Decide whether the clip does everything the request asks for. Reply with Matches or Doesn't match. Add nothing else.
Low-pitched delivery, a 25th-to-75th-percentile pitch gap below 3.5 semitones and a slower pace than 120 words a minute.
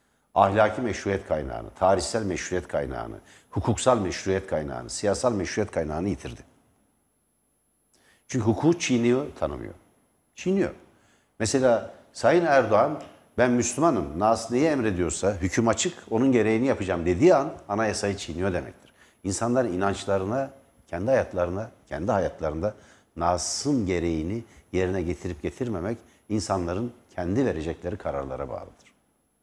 Doesn't match